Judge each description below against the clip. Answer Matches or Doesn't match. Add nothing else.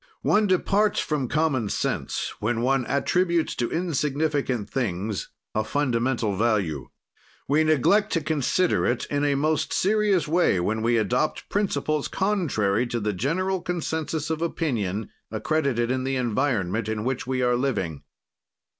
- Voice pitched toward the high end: Doesn't match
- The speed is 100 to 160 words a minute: Matches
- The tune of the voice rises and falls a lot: Matches